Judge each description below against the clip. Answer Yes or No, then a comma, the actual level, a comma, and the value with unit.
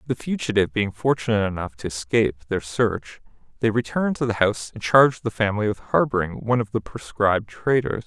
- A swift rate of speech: No, average, 185 wpm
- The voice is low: Yes, low, 110 Hz